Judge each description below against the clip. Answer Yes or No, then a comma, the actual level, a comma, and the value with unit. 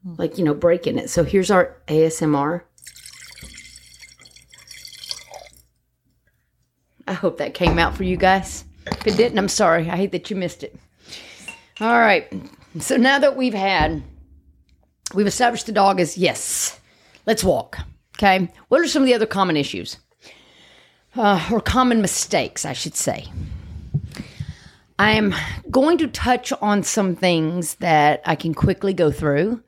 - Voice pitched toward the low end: No, high, 190 Hz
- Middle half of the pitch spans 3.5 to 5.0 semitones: No, wide, 5.4 semitones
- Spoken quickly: No, average, 150 wpm